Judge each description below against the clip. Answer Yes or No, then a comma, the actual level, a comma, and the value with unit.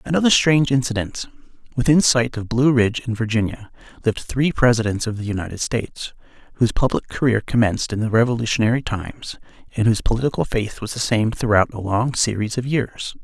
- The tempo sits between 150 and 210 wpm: Yes, average, 170 wpm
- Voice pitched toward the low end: Yes, low, 115 Hz